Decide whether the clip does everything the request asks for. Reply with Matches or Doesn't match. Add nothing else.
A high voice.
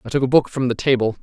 Doesn't match